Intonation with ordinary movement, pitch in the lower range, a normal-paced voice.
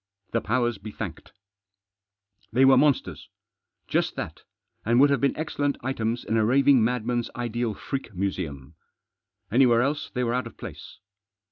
Yes: average, 3.1 semitones; low, 120 Hz; average, 150 wpm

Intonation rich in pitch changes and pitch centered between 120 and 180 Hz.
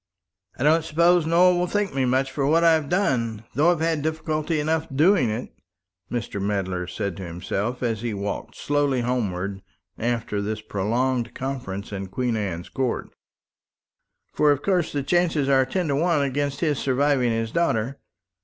Yes: wide, 6.1 semitones; low, 135 Hz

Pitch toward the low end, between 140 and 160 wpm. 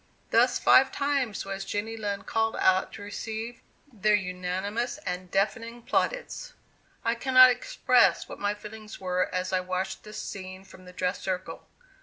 No: high, 205 Hz; average, 155 wpm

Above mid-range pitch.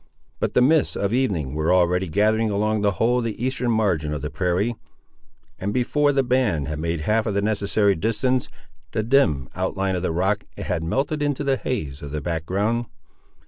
No: low, 105 Hz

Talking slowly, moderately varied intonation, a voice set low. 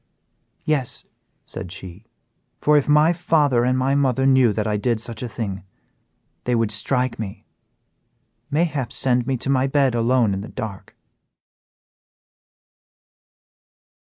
Yes: slow, 130 wpm; average, 3.7 semitones; low, 125 Hz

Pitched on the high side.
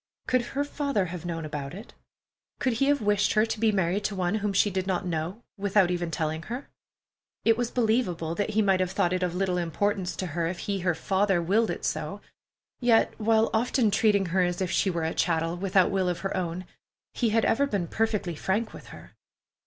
Yes: high, 195 Hz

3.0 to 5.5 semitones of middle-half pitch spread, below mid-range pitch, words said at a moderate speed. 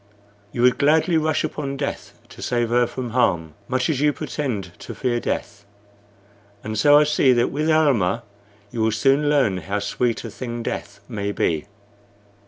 Yes: average, 5.0 semitones; low, 125 Hz; average, 175 wpm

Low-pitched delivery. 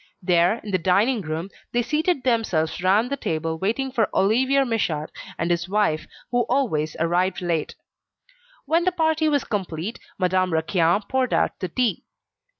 No: high, 200 Hz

